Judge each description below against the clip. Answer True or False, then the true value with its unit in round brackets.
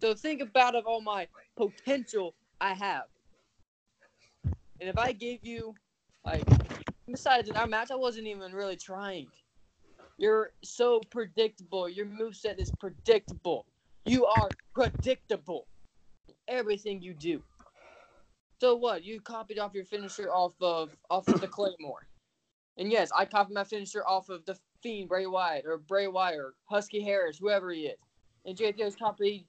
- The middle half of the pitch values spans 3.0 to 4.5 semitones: True (3.7 semitones)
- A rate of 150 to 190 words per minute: True (155 wpm)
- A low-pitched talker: False (205 Hz)